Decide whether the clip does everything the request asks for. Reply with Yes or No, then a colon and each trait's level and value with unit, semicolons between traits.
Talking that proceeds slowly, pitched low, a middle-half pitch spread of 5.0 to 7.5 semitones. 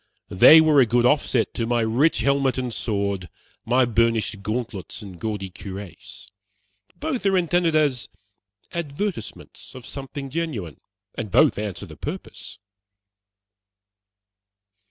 Yes: slow, 120 wpm; low, 120 Hz; wide, 5.6 semitones